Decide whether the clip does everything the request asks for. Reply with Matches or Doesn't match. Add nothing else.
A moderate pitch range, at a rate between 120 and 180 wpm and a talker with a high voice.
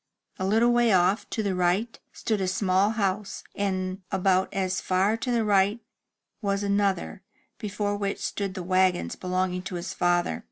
Doesn't match